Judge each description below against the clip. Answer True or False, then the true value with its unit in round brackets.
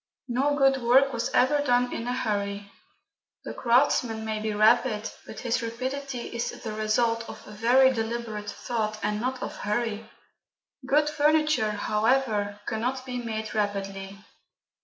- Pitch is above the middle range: True (230 Hz)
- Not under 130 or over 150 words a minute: True (140 wpm)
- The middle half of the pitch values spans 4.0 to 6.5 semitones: False (3.2 semitones)